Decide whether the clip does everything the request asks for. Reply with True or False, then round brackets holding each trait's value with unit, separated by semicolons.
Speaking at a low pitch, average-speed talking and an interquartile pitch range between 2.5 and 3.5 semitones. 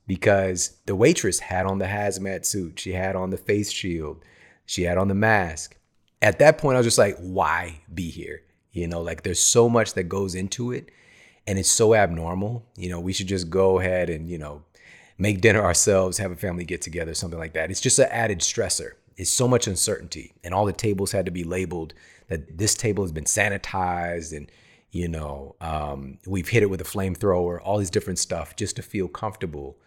False (95 Hz; 210 wpm; 2.9 semitones)